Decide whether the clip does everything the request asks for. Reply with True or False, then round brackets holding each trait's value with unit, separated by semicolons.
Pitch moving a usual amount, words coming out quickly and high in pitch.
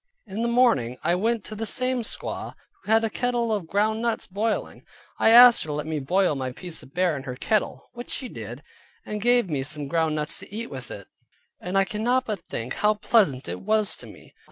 False (7.2 semitones; 225 wpm; 200 Hz)